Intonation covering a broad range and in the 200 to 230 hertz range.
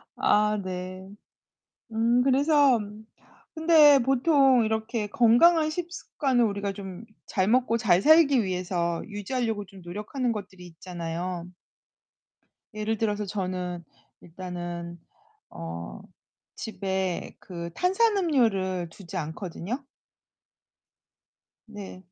Yes: wide, 5.7 semitones; high, 205 Hz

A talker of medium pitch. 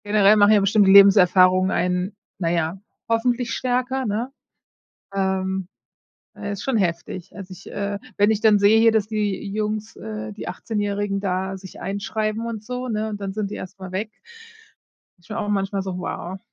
No: high, 200 Hz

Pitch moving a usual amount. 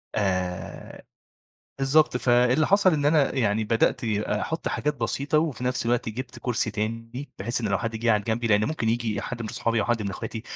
Yes: average, 3.4 semitones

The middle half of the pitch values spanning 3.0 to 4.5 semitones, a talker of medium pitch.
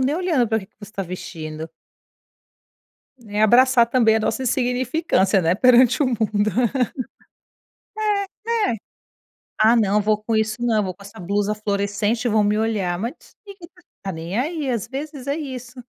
No: average, 3.9 semitones; high, 220 Hz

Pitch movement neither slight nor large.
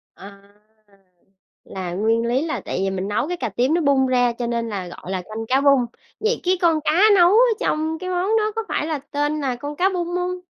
No: wide, 7.3 semitones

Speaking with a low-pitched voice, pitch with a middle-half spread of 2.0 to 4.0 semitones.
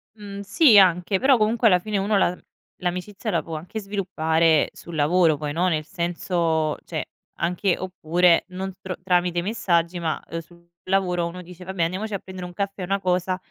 No: medium, 180 Hz; narrow, 2.4 semitones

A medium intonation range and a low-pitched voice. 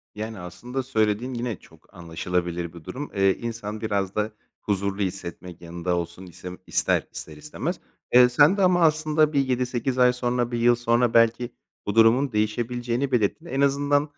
Yes: average, 4.7 semitones; low, 115 Hz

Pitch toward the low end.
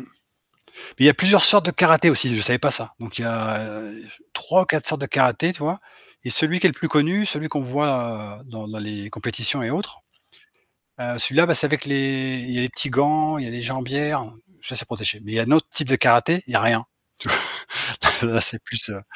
Yes: low, 130 Hz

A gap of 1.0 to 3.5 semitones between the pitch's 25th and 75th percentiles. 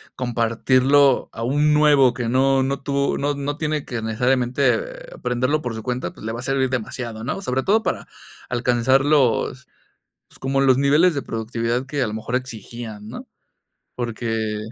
Yes: average, 3.0 semitones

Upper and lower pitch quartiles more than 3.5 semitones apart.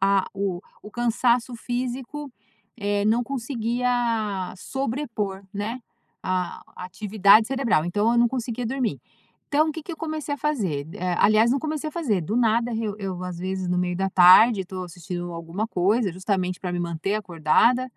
Yes: average, 4.9 semitones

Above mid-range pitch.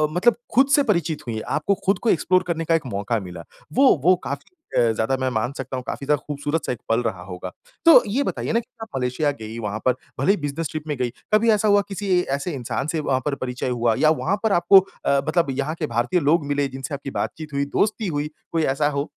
No: medium, 145 Hz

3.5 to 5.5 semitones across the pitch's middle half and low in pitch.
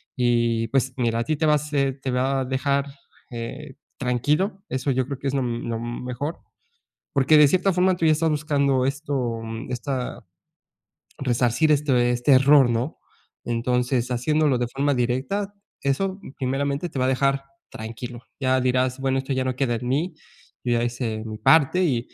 No: average, 2.9 semitones; low, 130 Hz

